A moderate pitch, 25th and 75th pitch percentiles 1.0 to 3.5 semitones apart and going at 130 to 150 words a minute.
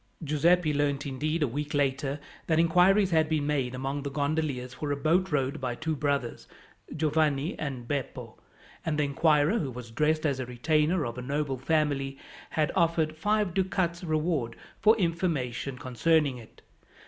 No: medium, 150 Hz; average, 2.9 semitones; average, 160 wpm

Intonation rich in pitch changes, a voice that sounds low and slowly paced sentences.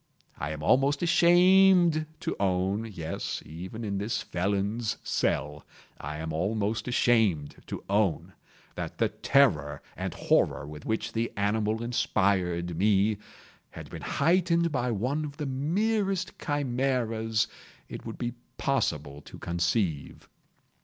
Yes: wide, 7.4 semitones; low, 110 Hz; slow, 120 wpm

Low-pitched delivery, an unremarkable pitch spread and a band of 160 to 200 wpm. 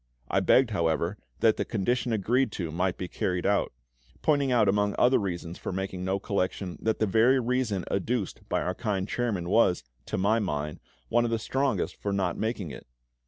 Yes: low, 100 Hz; average, 4.1 semitones; average, 190 wpm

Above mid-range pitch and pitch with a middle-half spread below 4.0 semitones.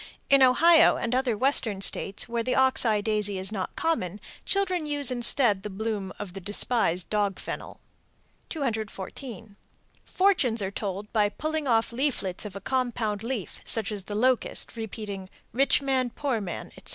No: high, 225 Hz; average, 4.5 semitones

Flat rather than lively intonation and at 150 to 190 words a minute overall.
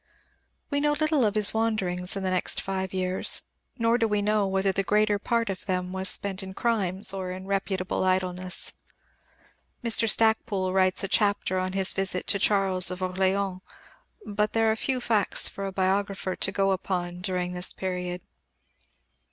Yes: narrow, 2.2 semitones; average, 170 wpm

